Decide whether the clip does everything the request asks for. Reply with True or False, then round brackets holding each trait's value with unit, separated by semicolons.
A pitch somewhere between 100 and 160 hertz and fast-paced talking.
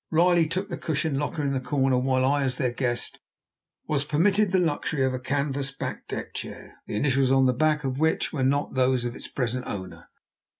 True (135 Hz; 210 wpm)